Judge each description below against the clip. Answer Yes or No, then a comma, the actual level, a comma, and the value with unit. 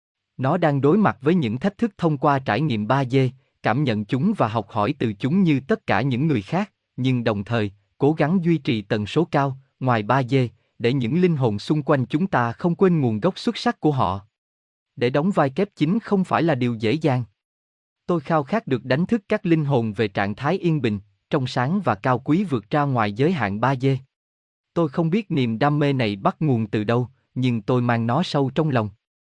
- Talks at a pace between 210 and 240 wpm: Yes, average, 225 wpm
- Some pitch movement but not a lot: No, wide, 5.8 semitones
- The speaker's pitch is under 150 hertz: Yes, low, 135 Hz